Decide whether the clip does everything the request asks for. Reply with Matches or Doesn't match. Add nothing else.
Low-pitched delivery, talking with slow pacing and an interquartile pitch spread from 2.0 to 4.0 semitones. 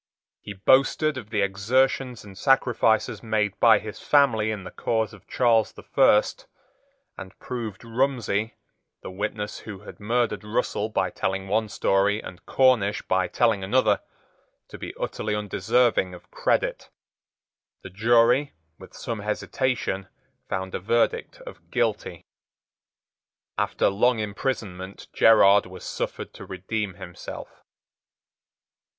Matches